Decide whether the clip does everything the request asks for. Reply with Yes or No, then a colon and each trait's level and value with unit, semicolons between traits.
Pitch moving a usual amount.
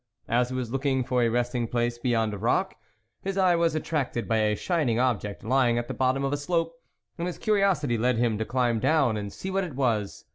Yes: average, 4.9 semitones